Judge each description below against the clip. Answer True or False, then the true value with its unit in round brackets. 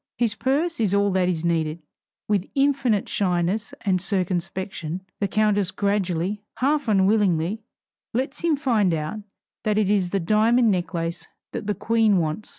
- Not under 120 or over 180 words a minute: True (150 wpm)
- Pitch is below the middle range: False (200 Hz)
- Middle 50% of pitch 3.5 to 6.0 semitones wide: True (3.8 semitones)